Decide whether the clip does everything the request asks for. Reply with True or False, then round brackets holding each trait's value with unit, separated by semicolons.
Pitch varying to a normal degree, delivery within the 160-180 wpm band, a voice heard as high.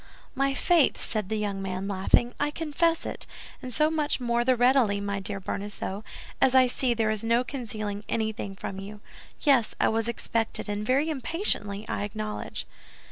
True (4.3 semitones; 175 wpm; 225 Hz)